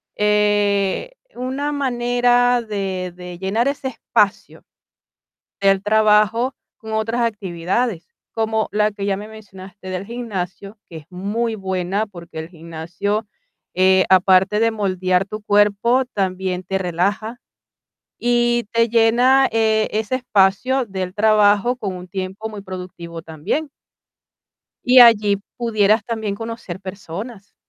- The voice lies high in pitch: Yes, high, 205 Hz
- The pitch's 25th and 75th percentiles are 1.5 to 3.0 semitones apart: No, average, 3.5 semitones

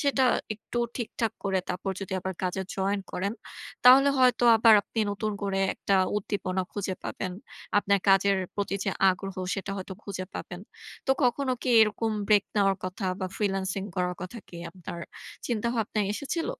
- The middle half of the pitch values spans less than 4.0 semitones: Yes, average, 2.9 semitones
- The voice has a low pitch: No, high, 200 Hz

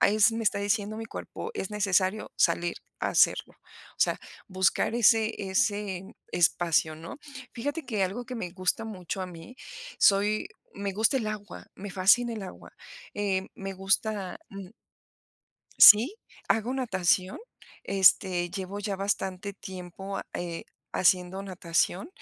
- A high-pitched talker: Yes, high, 195 Hz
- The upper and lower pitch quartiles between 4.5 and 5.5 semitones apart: No, average, 2.7 semitones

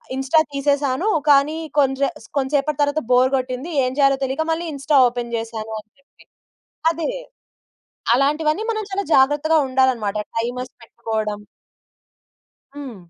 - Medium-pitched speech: No, very high, 270 Hz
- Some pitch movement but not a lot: Yes, average, 3.1 semitones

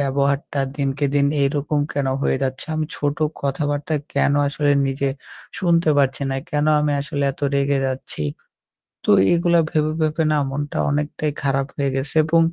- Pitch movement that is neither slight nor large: No, narrow, 1.6 semitones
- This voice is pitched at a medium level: Yes, medium, 145 Hz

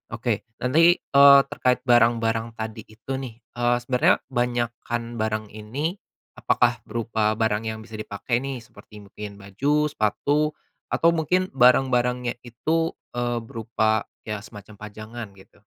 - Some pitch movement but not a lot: Yes, average, 3.1 semitones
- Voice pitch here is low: Yes, low, 120 Hz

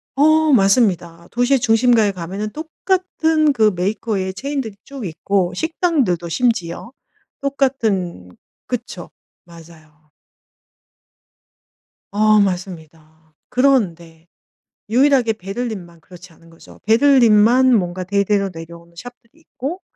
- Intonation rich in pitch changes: Yes, wide, 6.8 semitones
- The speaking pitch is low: No, high, 210 Hz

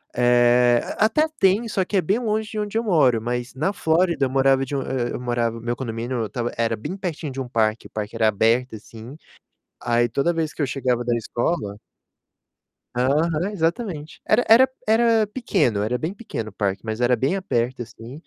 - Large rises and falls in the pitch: Yes, wide, 7.6 semitones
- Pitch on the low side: Yes, low, 130 Hz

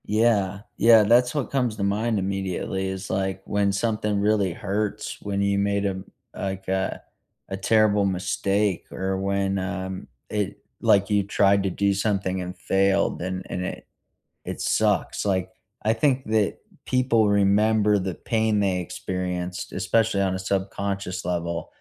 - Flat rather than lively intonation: Yes, narrow, 1.8 semitones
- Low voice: Yes, low, 100 Hz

